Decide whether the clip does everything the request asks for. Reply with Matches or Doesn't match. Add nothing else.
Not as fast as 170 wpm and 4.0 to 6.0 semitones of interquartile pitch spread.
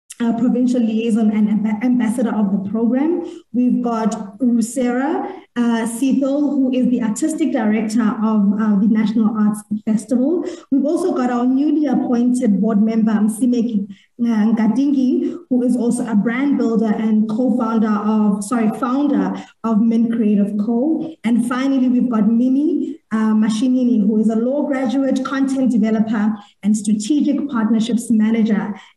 Doesn't match